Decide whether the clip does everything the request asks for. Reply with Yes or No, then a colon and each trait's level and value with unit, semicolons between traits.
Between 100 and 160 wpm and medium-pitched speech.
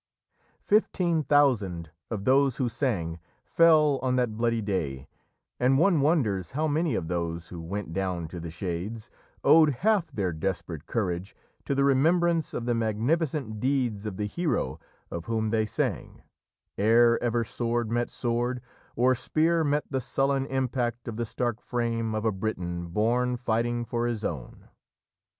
No: average, 155 wpm; low, 120 Hz